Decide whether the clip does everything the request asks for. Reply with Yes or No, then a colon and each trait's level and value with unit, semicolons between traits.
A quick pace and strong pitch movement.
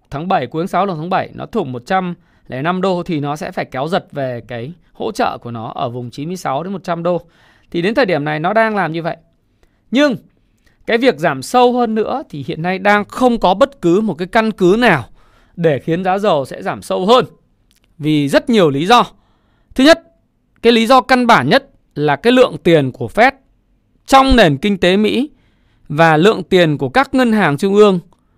No: average, 215 wpm; wide, 6.5 semitones